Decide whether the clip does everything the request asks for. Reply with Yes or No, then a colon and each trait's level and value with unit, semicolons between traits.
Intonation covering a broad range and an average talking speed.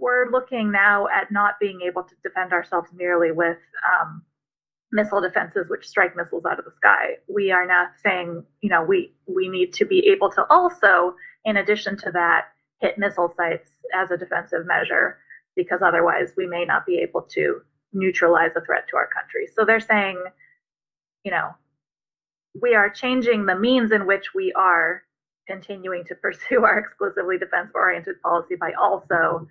Yes: wide, 6.2 semitones; average, 175 wpm